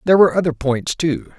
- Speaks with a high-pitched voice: No, medium, 160 Hz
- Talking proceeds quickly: Yes, fast, 215 wpm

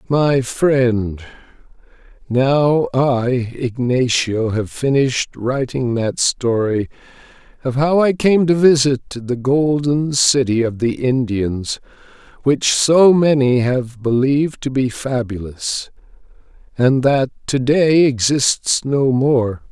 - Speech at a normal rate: No, slow, 115 wpm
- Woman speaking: No, male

